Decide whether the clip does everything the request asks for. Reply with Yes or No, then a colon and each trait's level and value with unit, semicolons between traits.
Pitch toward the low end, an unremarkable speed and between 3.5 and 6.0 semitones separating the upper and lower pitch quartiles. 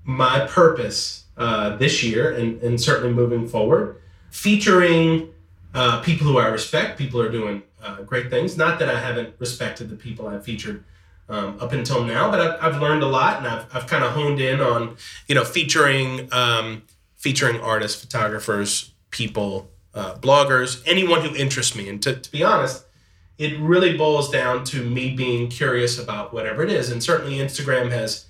Yes: low, 120 Hz; average, 180 wpm; average, 4.6 semitones